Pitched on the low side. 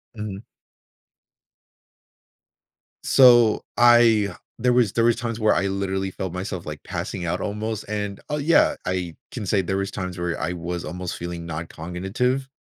Yes: low, 100 Hz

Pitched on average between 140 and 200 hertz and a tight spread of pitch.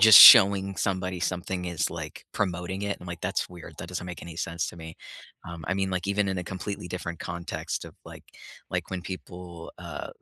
No: very low, 90 Hz; narrow, 1.9 semitones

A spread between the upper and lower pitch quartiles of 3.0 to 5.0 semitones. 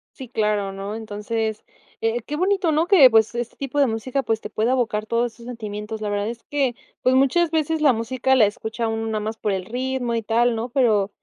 Yes: average, 3.3 semitones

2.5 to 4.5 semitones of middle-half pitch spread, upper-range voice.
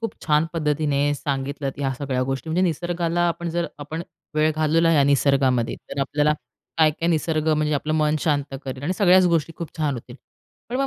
No: average, 2.9 semitones; medium, 155 Hz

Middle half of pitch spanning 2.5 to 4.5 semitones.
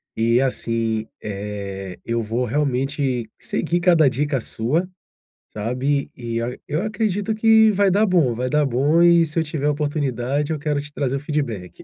No: wide, 5.4 semitones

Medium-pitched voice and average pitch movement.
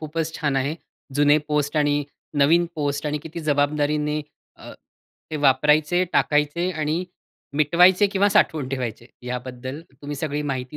No: medium, 150 Hz; narrow, 1.9 semitones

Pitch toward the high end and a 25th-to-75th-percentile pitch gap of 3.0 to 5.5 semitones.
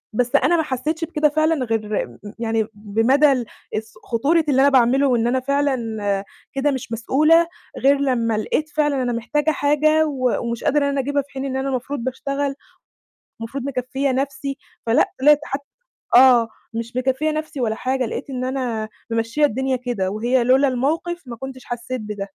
Yes: very high, 265 Hz; average, 3.3 semitones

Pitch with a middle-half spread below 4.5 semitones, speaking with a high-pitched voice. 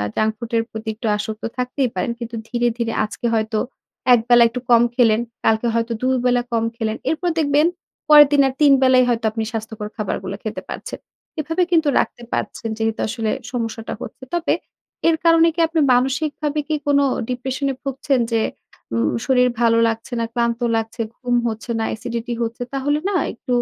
Yes: average, 3.5 semitones; high, 240 Hz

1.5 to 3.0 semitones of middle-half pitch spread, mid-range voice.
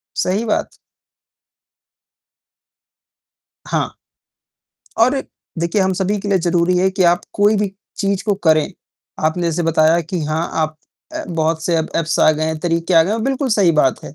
No: average, 3.6 semitones; medium, 175 Hz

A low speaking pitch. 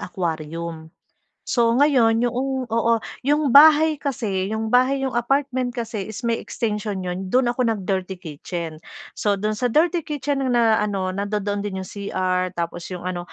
No: high, 220 Hz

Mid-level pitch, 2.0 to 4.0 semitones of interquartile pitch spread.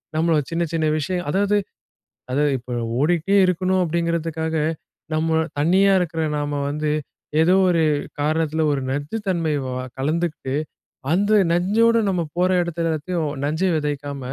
Yes: medium, 165 Hz; average, 3.2 semitones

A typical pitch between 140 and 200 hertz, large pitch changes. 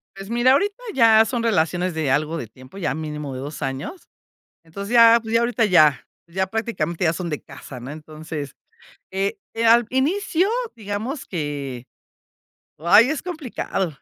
Yes: medium, 185 Hz; wide, 7.4 semitones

